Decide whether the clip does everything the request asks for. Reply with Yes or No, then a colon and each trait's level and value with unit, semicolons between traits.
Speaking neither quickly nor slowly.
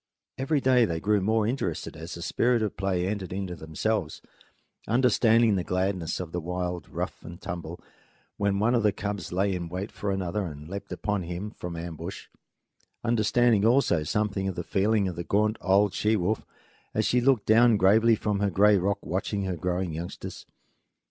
Yes: average, 180 wpm